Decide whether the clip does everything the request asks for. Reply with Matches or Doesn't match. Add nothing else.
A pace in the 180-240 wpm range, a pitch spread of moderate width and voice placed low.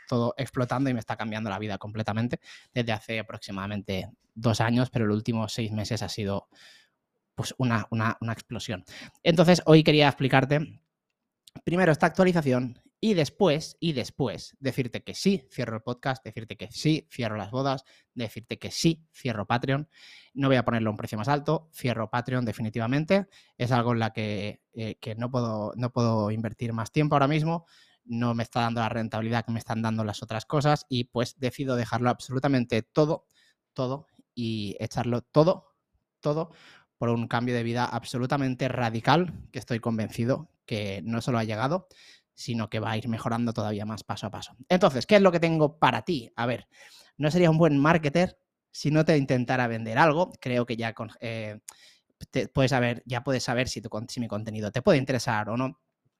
Matches